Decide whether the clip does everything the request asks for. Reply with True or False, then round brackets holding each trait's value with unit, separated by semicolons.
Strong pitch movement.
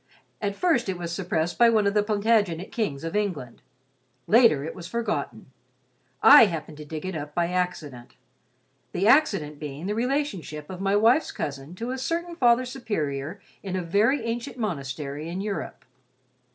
True (6.7 semitones)